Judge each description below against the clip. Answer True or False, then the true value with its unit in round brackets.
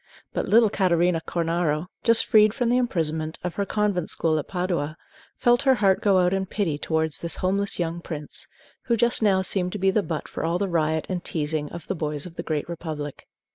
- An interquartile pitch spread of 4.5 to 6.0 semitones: False (4.0 semitones)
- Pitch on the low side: False (175 Hz)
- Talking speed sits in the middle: False (215 wpm)